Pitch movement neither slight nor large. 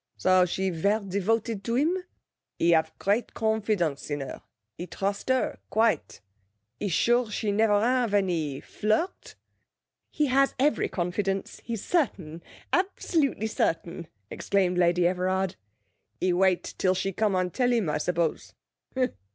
Yes: average, 4.1 semitones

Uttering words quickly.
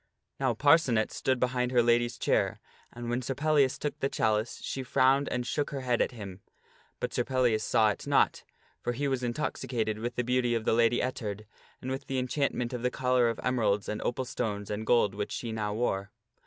Yes: fast, 210 wpm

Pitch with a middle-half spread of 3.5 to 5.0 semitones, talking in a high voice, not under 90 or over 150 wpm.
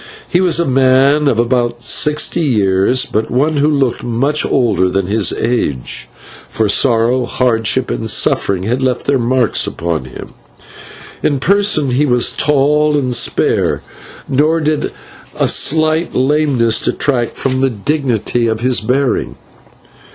No: average, 4.2 semitones; low, 130 Hz; average, 140 wpm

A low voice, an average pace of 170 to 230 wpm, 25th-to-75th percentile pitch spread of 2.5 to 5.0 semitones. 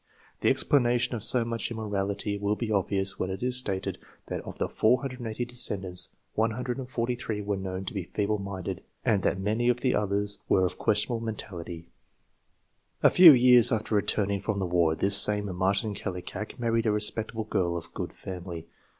Yes: low, 105 Hz; average, 175 wpm; average, 3.3 semitones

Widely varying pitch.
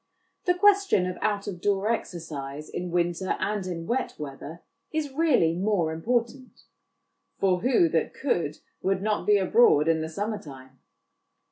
Yes: wide, 5.8 semitones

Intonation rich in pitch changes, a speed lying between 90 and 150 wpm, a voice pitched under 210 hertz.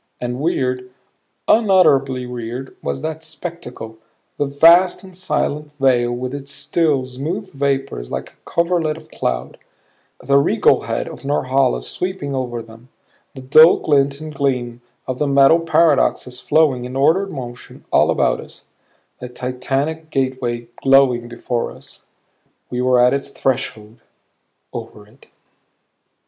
No: average, 3.8 semitones; slow, 135 wpm; low, 135 Hz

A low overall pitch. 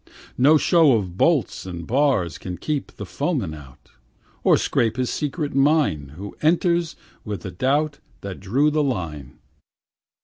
Yes: low, 130 Hz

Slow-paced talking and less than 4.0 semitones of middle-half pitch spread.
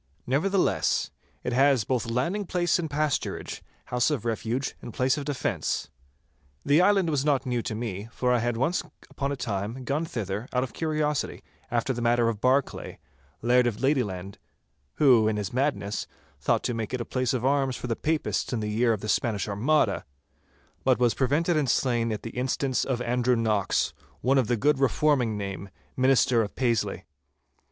No: average, 180 wpm; average, 3.6 semitones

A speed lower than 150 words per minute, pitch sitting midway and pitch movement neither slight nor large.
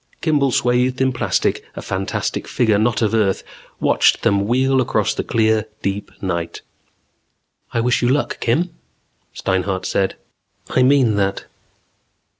No: slow, 135 wpm; low, 115 Hz; average, 4.4 semitones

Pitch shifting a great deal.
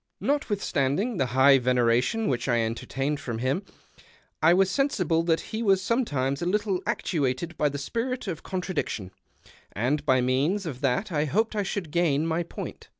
Yes: wide, 6.6 semitones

